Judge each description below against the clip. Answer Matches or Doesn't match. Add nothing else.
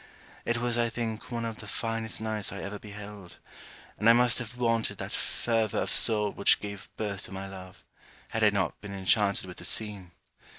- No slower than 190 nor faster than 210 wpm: Matches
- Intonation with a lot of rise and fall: Doesn't match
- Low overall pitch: Matches